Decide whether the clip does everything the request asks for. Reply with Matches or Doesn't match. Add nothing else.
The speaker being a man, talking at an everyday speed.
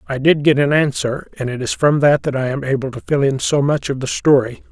Doesn't match